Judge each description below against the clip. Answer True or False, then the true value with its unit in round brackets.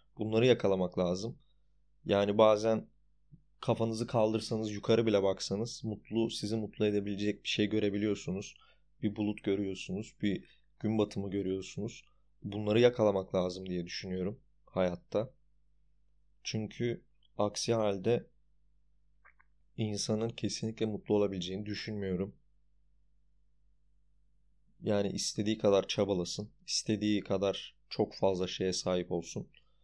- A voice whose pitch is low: True (105 Hz)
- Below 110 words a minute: True (100 wpm)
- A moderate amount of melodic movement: False (2.2 semitones)